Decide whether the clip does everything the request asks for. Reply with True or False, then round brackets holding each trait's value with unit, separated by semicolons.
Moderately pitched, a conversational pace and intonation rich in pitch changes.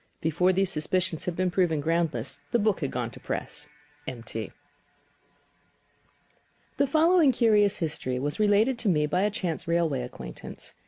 True (175 Hz; 160 wpm; 5.7 semitones)